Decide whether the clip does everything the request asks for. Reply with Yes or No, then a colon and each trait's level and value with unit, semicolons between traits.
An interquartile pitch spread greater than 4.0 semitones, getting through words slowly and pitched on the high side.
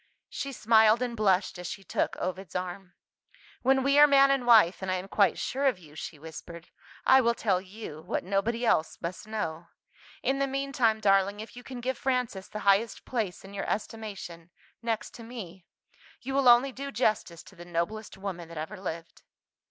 No: average, 5.1 semitones; average, 190 wpm; high, 210 Hz